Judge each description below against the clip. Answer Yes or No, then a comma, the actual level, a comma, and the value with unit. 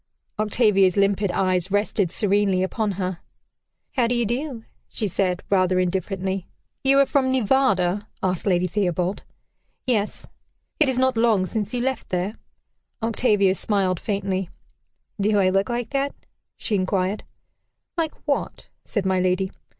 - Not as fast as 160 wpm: Yes, average, 140 wpm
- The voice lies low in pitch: No, high, 200 Hz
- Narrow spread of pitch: No, average, 3.9 semitones